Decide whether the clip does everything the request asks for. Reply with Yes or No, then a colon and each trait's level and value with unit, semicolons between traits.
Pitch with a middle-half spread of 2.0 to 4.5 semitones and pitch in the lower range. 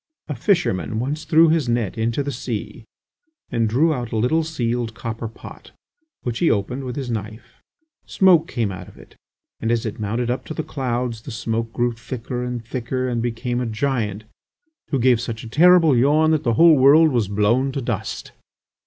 Yes: average, 3.7 semitones; low, 120 Hz